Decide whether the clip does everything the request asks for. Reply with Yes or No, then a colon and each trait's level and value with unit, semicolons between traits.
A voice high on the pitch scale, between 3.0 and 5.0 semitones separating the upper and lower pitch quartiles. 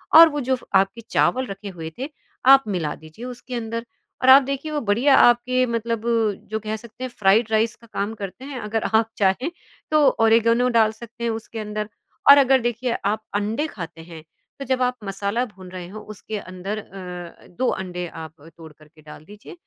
Yes: high, 220 Hz; average, 4.4 semitones